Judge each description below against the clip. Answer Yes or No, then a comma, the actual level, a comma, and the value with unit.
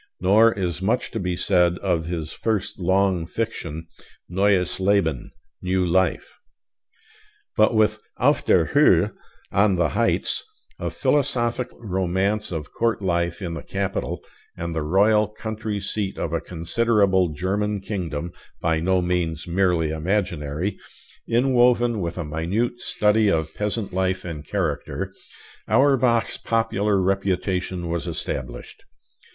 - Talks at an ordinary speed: No, slow, 125 wpm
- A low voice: Yes, very low, 95 Hz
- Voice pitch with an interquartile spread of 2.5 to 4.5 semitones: Yes, average, 3.6 semitones